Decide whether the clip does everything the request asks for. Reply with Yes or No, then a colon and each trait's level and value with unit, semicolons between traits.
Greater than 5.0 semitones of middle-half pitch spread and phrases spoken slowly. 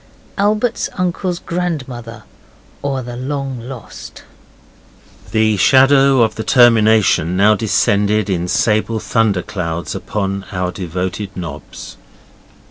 Yes: wide, 5.4 semitones; slow, 105 wpm